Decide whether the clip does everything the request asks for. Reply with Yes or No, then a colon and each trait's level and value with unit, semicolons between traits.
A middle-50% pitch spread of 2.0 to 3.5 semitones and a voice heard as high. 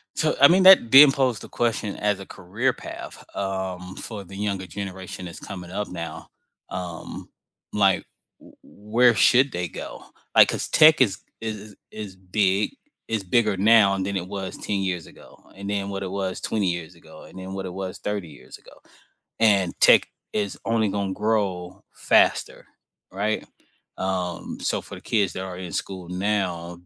No: narrow, 2.5 semitones; low, 100 Hz